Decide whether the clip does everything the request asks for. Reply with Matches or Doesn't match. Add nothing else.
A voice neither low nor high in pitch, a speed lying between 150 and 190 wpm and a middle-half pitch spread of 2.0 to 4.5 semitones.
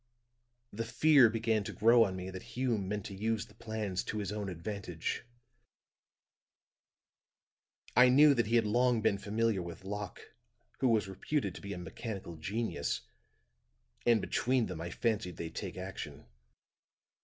Doesn't match